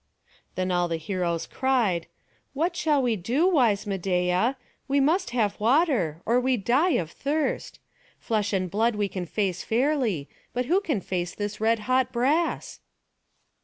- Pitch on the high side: Yes, high, 225 Hz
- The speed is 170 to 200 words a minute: No, average, 155 wpm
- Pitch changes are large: Yes, wide, 6.4 semitones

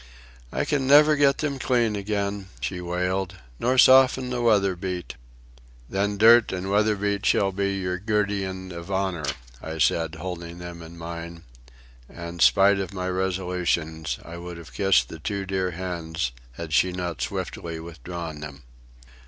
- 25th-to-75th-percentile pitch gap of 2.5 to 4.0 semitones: Yes, average, 3.1 semitones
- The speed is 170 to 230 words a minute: No, average, 155 wpm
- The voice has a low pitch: Yes, very low, 95 Hz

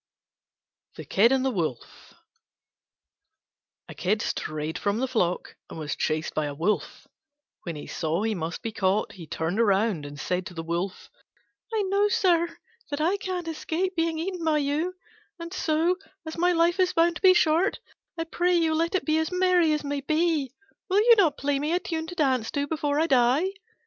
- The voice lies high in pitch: Yes, very high, 305 Hz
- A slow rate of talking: No, average, 195 wpm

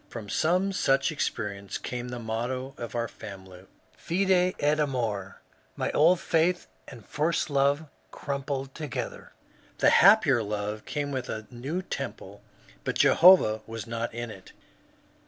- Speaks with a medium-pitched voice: No, low, 130 Hz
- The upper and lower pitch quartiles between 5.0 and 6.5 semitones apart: Yes, wide, 5.6 semitones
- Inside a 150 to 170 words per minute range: No, average, 140 wpm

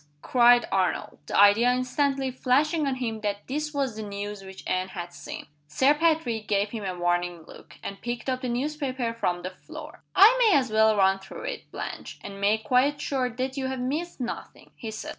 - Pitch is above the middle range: Yes, high, 240 Hz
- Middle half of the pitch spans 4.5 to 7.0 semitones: Yes, average, 5.1 semitones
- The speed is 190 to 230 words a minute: Yes, average, 200 wpm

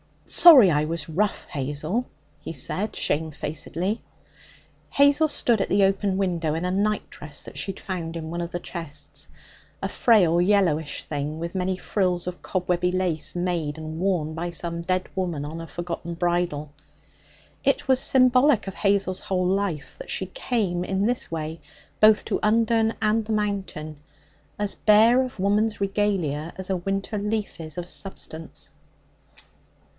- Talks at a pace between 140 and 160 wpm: Yes, average, 155 wpm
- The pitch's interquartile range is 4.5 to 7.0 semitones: No, average, 4.1 semitones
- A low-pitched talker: No, medium, 185 Hz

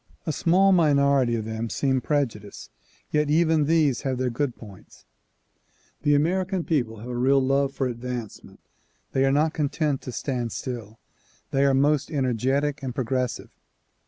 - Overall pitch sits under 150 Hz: Yes, low, 135 Hz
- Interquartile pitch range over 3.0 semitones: Yes, average, 3.4 semitones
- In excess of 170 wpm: No, average, 155 wpm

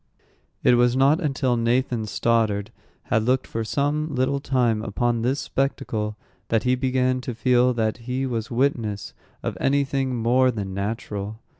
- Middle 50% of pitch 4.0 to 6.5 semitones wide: No, average, 2.7 semitones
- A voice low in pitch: Yes, low, 125 Hz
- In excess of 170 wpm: No, average, 155 wpm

